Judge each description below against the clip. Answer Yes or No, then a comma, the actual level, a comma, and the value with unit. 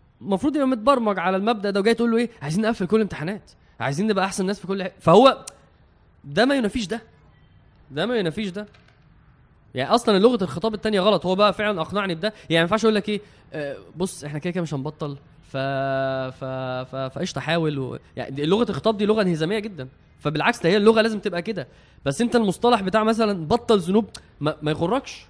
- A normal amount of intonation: No, wide, 6.3 semitones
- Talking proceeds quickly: Yes, fast, 200 wpm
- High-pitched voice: Yes, high, 195 Hz